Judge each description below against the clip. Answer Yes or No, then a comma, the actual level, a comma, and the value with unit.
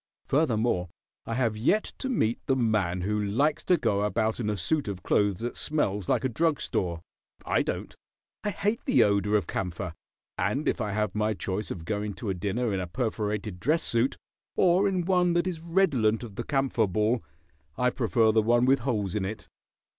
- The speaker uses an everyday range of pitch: Yes, average, 5.0 semitones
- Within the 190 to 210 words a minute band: Yes, average, 200 wpm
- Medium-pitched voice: No, low, 110 Hz